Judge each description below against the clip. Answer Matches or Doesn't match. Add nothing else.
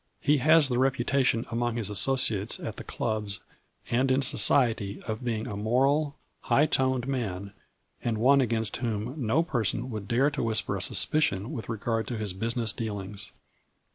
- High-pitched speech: Doesn't match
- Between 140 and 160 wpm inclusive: Doesn't match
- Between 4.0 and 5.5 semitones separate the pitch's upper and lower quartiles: Doesn't match